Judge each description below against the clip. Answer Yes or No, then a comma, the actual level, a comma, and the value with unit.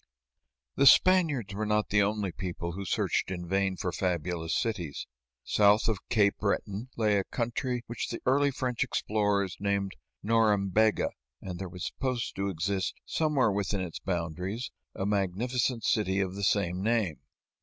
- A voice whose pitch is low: Yes, low, 100 Hz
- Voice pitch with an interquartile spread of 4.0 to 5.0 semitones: No, average, 3.4 semitones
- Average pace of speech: Yes, average, 155 wpm